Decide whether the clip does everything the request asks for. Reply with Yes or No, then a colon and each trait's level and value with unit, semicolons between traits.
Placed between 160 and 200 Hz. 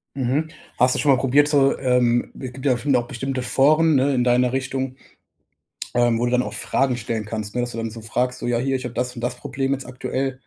No: low, 125 Hz